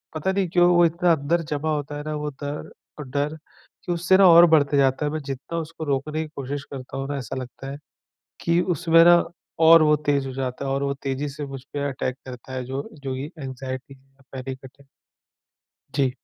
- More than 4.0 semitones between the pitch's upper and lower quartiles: No, average, 2.9 semitones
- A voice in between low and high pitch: Yes, medium, 145 Hz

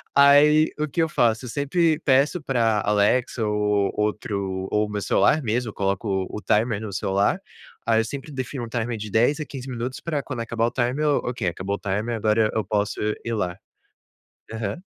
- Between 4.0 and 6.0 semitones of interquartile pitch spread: Yes, average, 4.4 semitones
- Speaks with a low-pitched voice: Yes, low, 115 Hz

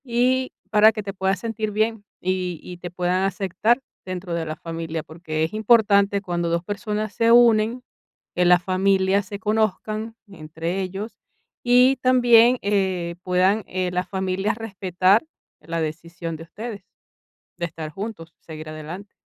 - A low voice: No, high, 190 Hz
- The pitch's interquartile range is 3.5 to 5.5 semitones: Yes, average, 3.8 semitones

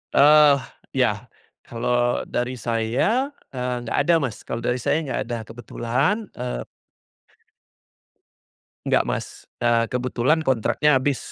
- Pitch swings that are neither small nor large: Yes, average, 3.0 semitones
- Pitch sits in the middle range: No, low, 125 Hz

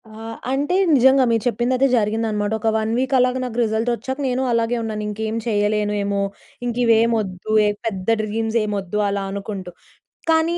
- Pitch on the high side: Yes, high, 225 Hz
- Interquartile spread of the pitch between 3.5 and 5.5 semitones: No, average, 2.9 semitones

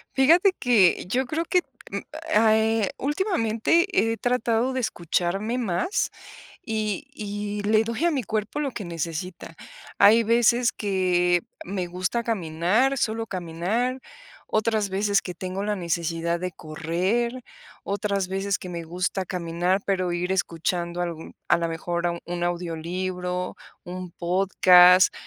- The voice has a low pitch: No, high, 195 Hz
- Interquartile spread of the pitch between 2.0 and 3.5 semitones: No, average, 4.4 semitones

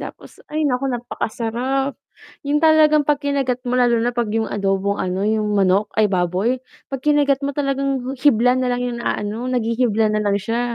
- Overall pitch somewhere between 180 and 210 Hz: No, high, 245 Hz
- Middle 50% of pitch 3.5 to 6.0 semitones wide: Yes, average, 4.2 semitones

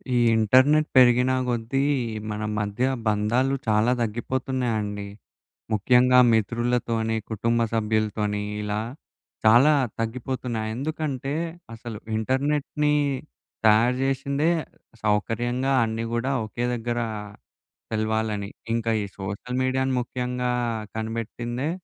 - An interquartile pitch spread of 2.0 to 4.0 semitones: Yes, average, 2.8 semitones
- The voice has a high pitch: No, low, 120 Hz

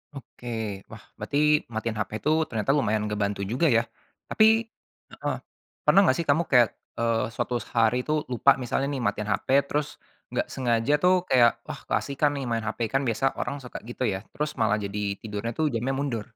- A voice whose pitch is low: Yes, low, 120 Hz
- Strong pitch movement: No, average, 4.0 semitones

